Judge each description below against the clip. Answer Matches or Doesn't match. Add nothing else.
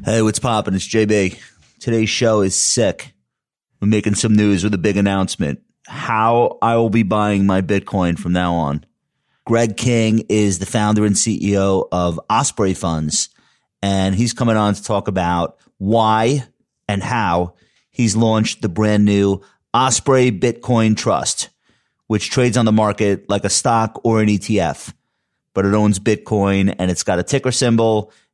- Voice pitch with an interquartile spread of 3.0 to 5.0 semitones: Doesn't match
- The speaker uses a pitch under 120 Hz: Matches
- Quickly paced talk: Doesn't match